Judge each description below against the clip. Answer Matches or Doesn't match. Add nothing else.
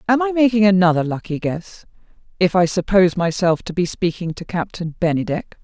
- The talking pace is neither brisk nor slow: Matches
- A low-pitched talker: Doesn't match